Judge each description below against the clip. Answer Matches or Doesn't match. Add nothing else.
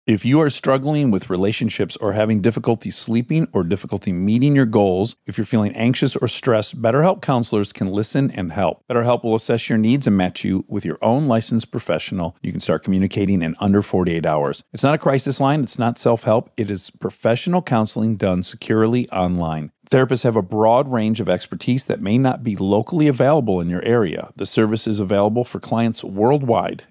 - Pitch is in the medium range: Doesn't match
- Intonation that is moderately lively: Matches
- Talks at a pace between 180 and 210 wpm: Matches